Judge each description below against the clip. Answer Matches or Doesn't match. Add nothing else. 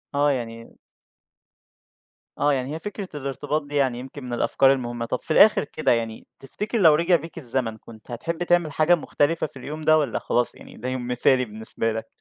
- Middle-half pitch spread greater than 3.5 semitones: Matches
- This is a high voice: Doesn't match